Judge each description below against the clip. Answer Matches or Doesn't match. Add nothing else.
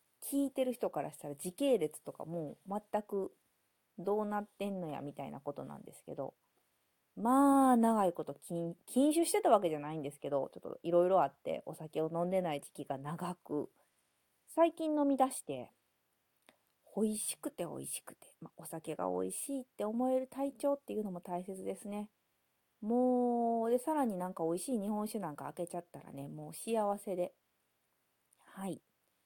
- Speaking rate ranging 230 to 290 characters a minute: Doesn't match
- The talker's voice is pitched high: Matches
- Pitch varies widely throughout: Matches